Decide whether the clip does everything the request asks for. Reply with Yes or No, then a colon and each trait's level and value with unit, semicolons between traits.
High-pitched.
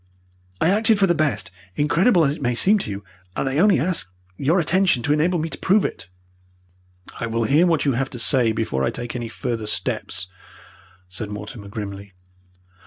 No: low, 135 Hz